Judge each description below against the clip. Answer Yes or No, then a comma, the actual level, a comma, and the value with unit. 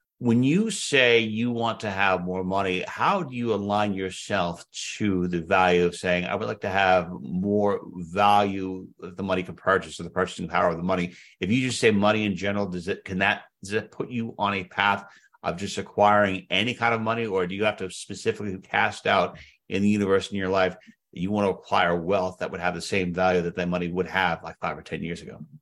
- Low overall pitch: Yes, low, 100 Hz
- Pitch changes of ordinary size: No, narrow, 2.2 semitones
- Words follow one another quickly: Yes, fast, 235 wpm